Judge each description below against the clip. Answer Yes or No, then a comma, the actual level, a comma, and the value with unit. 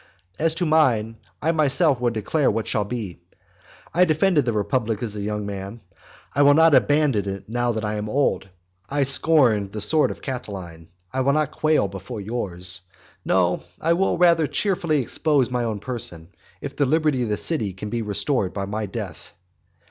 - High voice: No, low, 120 Hz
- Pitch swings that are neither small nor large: No, wide, 6.6 semitones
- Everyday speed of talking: Yes, average, 185 wpm